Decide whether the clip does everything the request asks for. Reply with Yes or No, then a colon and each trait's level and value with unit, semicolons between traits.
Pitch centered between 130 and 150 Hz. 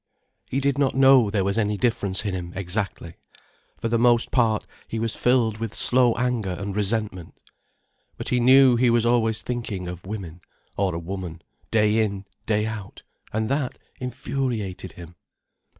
No: low, 110 Hz